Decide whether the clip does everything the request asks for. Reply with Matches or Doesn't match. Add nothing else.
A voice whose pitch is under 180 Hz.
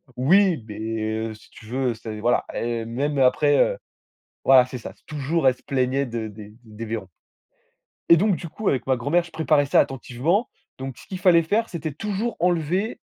Matches